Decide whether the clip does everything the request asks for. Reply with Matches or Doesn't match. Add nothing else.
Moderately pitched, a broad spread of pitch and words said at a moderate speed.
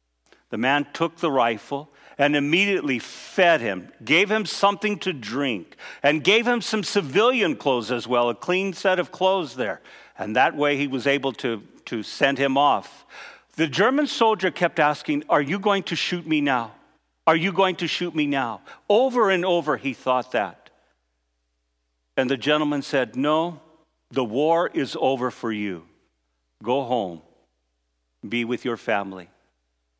Matches